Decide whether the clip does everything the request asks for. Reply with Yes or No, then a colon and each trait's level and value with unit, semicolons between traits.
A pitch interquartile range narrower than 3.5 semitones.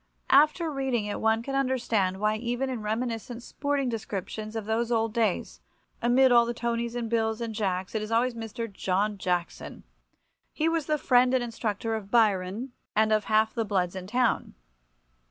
Yes: narrow, 2.5 semitones